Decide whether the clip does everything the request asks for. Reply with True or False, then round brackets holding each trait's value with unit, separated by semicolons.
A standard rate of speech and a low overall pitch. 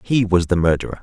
False (235 wpm; 95 Hz)